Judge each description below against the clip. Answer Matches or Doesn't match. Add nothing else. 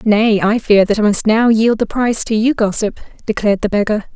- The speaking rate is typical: Doesn't match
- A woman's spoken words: Matches